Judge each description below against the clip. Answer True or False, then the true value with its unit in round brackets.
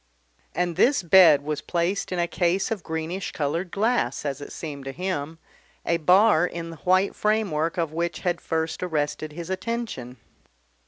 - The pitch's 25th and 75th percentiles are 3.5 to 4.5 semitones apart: False (3.1 semitones)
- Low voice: False (170 Hz)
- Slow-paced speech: False (165 wpm)